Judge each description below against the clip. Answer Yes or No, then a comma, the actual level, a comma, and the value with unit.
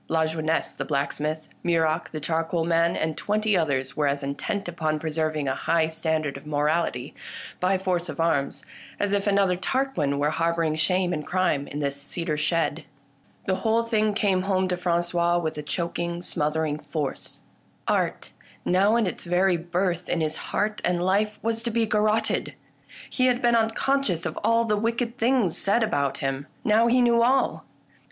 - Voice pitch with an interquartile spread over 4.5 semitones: Yes, average, 5.1 semitones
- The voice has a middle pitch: Yes, medium, 175 Hz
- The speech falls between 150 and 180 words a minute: Yes, average, 170 wpm